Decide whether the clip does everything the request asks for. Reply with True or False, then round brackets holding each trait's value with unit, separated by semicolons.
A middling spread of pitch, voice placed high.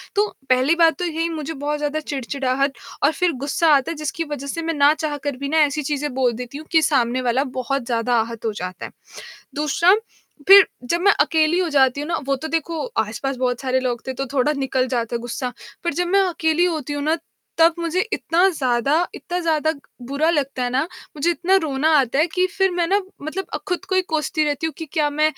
True (4.0 semitones; 295 Hz)